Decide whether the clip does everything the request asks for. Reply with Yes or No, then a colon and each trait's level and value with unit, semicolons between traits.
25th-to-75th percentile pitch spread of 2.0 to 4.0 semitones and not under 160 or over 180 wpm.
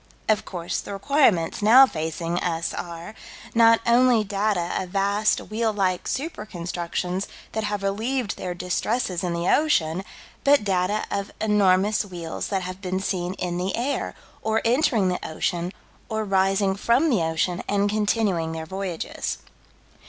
No: average, 3.5 semitones; average, 150 wpm